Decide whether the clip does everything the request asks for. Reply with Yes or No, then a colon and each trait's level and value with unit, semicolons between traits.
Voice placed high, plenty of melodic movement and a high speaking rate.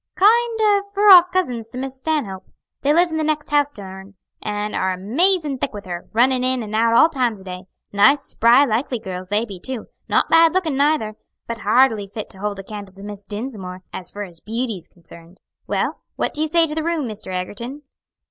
Yes: high, 230 Hz; wide, 6.9 semitones; fast, 215 wpm